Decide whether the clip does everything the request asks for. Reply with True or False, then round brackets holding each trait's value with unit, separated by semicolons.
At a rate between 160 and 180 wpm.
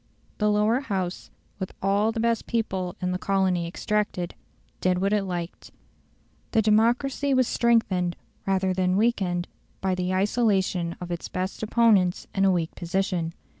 False (150 wpm)